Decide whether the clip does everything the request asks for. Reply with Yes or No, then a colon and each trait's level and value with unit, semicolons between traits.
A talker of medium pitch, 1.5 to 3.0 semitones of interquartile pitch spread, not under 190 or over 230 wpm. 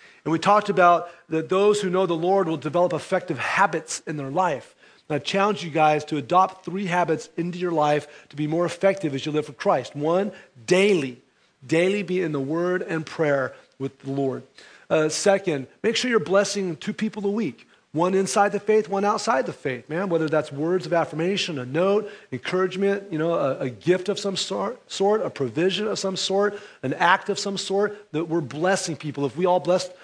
No: medium, 180 Hz; average, 4.1 semitones; average, 200 wpm